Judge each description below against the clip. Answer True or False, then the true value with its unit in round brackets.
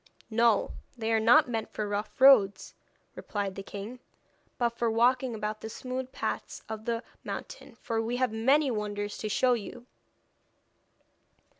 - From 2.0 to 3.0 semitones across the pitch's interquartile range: True (2.7 semitones)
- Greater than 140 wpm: True (150 wpm)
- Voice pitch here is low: False (225 Hz)